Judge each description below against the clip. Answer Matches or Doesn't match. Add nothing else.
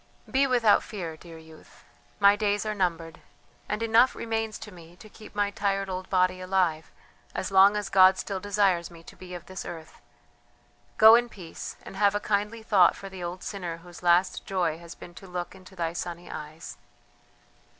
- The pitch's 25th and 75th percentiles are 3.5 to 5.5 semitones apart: Doesn't match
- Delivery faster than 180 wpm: Matches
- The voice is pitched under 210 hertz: Matches